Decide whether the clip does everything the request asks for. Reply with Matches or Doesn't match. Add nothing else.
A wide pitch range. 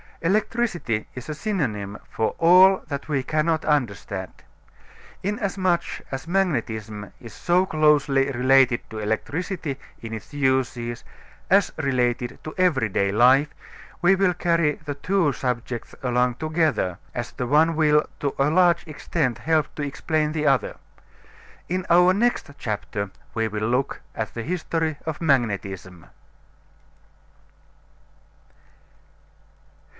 Matches